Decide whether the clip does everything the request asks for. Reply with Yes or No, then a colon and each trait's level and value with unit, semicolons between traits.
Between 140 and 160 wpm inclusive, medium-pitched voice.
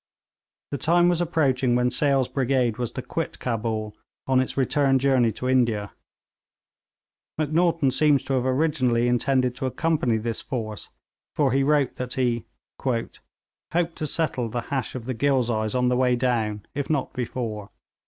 No: average, 155 wpm; low, 130 Hz